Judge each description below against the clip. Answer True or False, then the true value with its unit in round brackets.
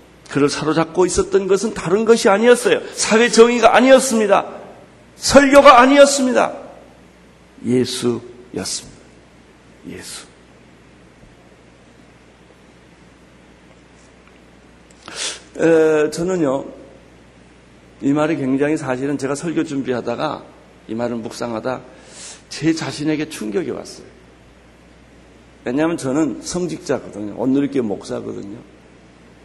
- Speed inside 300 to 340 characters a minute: False (220 characters per minute)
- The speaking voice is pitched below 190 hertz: True (140 Hz)